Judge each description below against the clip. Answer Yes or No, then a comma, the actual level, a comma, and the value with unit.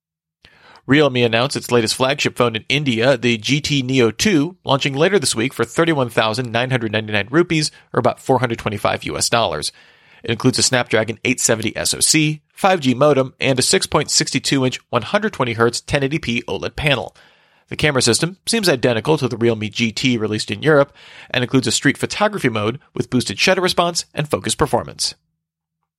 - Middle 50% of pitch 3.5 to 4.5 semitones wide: Yes, average, 4.1 semitones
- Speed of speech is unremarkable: Yes, average, 150 wpm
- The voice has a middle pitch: No, low, 125 Hz